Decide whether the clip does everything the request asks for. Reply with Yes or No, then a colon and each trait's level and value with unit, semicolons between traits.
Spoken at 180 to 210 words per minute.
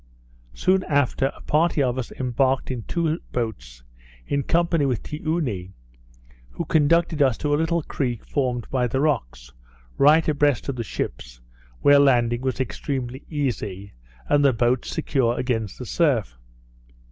No: average, 145 wpm